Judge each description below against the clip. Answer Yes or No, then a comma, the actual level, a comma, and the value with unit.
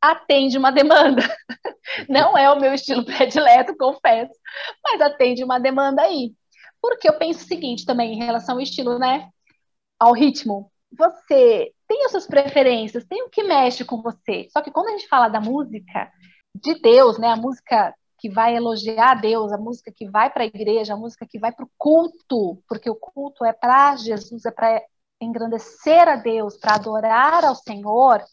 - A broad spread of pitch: No, average, 4.7 semitones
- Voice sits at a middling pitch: No, very high, 255 Hz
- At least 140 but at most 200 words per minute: Yes, average, 180 wpm